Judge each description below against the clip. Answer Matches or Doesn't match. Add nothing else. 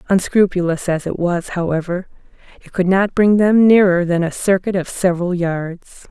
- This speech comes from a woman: Matches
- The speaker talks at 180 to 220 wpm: Doesn't match